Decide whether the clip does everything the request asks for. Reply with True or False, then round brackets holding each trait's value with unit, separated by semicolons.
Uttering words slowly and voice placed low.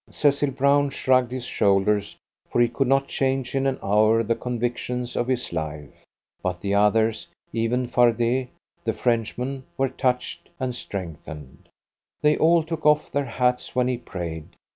False (155 wpm; 125 Hz)